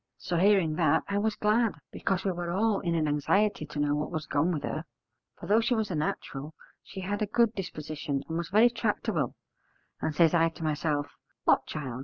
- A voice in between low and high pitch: Yes, medium, 170 Hz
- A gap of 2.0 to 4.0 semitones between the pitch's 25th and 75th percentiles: No, average, 5.0 semitones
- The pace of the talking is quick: Yes, fast, 210 wpm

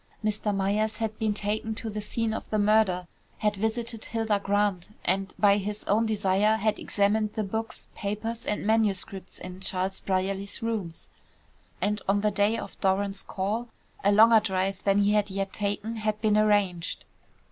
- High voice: Yes, high, 205 Hz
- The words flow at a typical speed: Yes, average, 170 wpm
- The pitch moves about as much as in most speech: No, narrow, 1.8 semitones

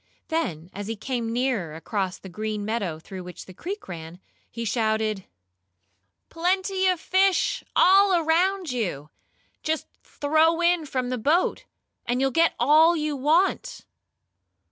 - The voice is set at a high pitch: Yes, very high, 260 Hz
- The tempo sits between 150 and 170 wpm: No, average, 140 wpm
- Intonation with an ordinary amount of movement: No, wide, 8.4 semitones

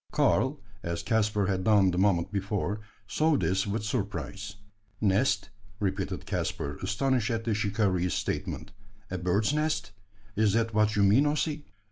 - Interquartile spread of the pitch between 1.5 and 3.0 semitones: Yes, average, 2.7 semitones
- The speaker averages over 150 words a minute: No, average, 145 wpm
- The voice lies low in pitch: Yes, low, 105 Hz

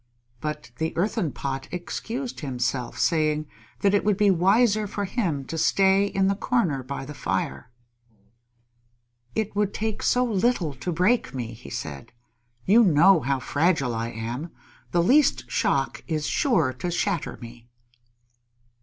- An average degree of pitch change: No, wide, 7.1 semitones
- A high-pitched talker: No, medium, 170 Hz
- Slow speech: No, average, 145 wpm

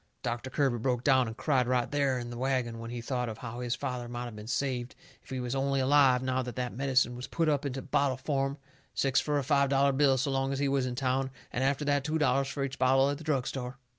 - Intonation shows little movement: Yes, narrow, 2.0 semitones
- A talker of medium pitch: No, low, 130 Hz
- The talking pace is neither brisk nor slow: No, fast, 265 wpm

